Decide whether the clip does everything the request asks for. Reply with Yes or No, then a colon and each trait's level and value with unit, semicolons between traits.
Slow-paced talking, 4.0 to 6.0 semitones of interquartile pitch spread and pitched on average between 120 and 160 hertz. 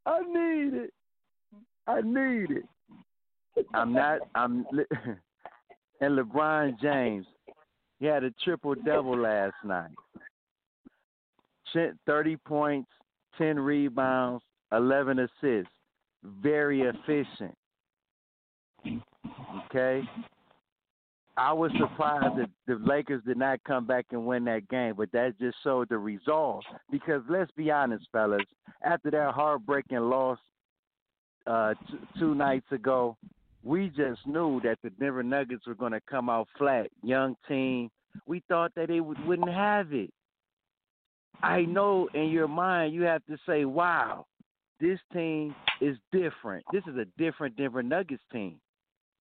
Yes: slow, 130 wpm; average, 4.8 semitones; medium, 140 Hz